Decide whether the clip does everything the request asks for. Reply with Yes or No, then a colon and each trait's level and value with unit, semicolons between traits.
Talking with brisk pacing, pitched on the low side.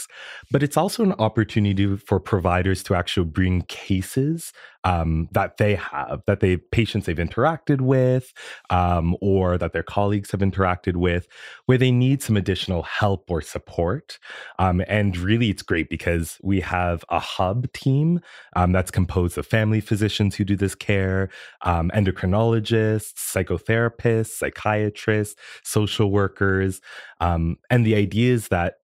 No: average, 145 wpm; low, 100 Hz